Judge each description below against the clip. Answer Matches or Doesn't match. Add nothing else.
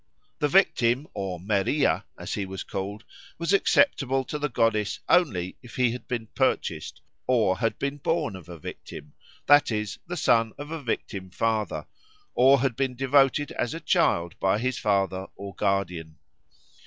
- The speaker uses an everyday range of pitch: Doesn't match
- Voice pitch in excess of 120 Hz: Doesn't match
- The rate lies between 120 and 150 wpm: Doesn't match